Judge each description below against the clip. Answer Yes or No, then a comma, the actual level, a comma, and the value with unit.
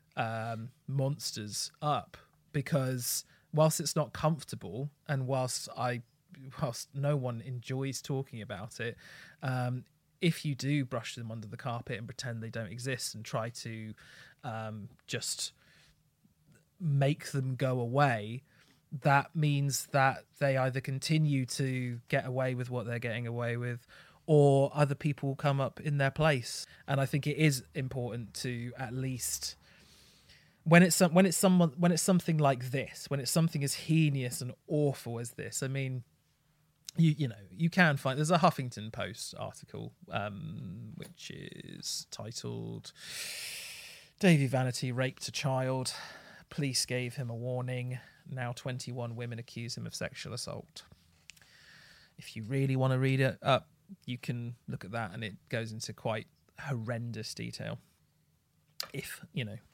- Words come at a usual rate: Yes, average, 155 wpm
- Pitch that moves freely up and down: No, average, 3.5 semitones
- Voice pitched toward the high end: No, low, 135 Hz